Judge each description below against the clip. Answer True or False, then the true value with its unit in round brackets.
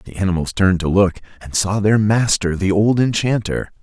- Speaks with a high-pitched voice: False (100 Hz)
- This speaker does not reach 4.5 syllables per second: False (5.2 syllables/s)